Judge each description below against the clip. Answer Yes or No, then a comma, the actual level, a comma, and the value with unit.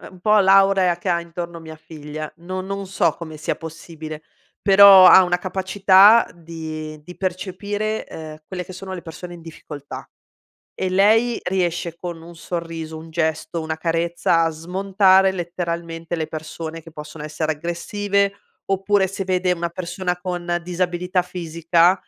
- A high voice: No, medium, 175 Hz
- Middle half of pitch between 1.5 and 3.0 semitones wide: Yes, narrow, 2.4 semitones